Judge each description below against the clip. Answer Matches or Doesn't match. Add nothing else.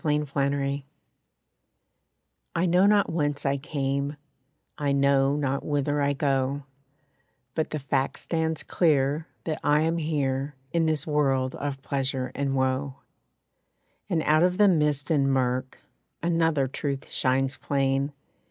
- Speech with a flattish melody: Matches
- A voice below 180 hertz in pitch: Matches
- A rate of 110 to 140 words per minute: Matches